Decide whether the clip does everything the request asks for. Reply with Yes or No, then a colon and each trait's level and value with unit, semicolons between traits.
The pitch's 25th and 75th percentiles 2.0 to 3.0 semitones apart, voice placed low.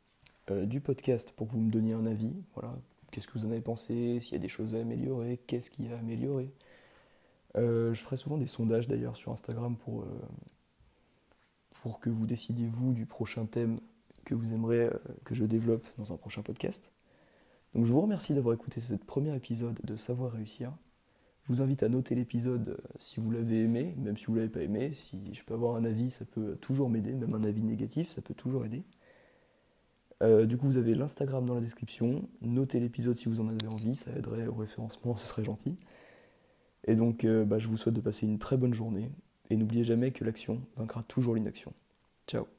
Yes: narrow, 2.4 semitones; low, 115 Hz